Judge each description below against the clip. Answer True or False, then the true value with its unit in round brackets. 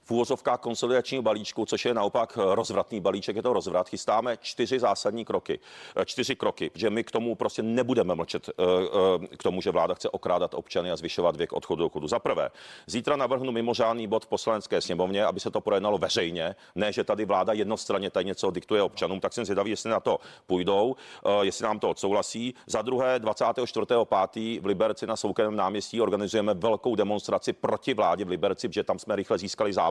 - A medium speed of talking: False (185 wpm)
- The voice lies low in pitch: True (125 Hz)